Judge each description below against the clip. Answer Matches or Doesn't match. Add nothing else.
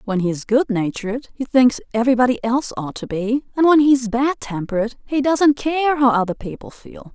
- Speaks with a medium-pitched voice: Doesn't match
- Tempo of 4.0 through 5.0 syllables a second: Doesn't match